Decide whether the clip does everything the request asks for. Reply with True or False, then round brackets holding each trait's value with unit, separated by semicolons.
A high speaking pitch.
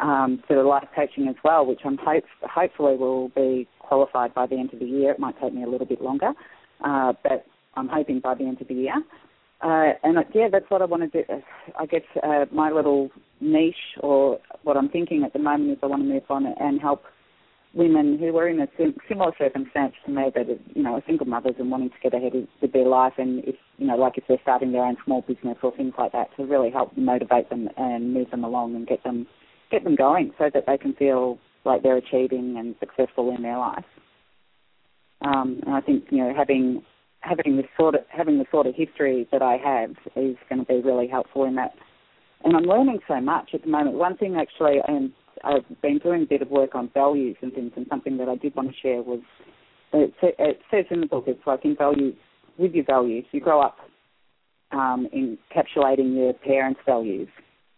False (135 Hz)